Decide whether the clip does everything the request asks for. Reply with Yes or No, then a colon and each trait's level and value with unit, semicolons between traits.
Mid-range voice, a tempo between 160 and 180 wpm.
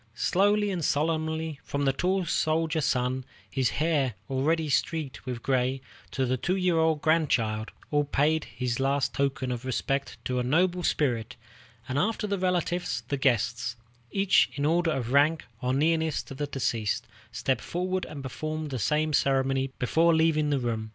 Yes: medium, 145 Hz; average, 170 wpm